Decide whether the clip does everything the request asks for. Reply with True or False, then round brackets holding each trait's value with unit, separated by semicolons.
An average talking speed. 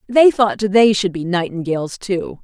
True (170 wpm)